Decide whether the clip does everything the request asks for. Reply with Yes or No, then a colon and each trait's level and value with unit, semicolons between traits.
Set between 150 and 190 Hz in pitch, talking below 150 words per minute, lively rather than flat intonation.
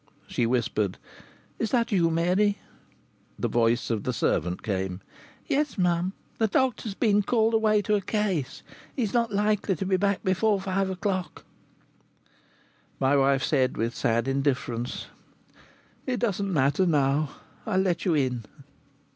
Yes: medium, 185 Hz; average, 140 wpm; wide, 7.6 semitones